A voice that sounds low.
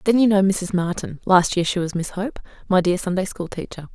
No: medium, 185 Hz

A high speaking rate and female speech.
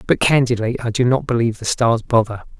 No: fast, 210 wpm; male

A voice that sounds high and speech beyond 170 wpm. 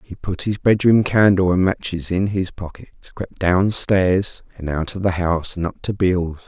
No: very low, 95 Hz; fast, 205 wpm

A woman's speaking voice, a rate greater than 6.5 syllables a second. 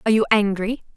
Yes: female; 7.3 syllables/s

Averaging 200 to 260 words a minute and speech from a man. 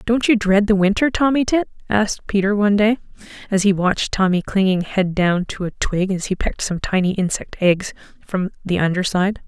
No: fast, 205 wpm; female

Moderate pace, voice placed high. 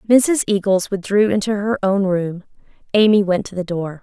Yes: average, 180 wpm; high, 200 Hz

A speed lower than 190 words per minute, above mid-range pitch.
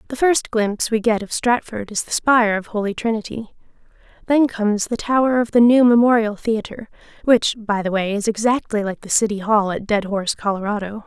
No: average, 195 wpm; high, 220 Hz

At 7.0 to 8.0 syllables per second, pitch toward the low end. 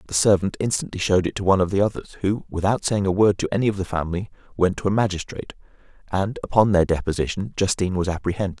Yes: 7.1 syllables/s; very low, 95 Hz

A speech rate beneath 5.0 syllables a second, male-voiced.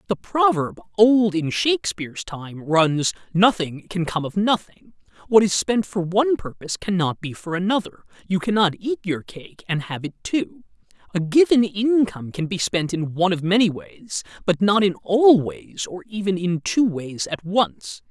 Yes: 4.6 syllables/s; male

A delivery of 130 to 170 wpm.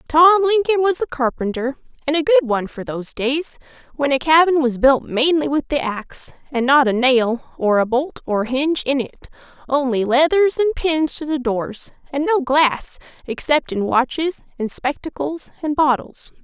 No: average, 180 wpm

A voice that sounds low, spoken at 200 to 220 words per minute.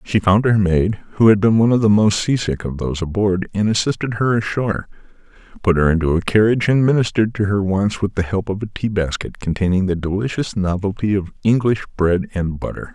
Yes: low, 100 Hz; fast, 205 wpm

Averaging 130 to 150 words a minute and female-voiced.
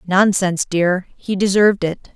Yes: average, 140 wpm; female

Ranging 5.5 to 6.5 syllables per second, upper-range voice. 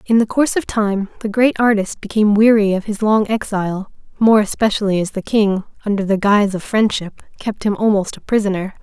Yes: 5.8 syllables/s; high, 210 Hz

